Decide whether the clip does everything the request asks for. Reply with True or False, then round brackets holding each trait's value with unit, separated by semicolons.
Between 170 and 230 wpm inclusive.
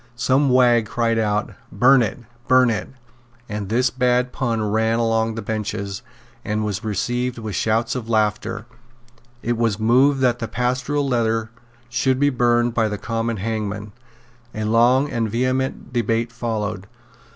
False (150 wpm)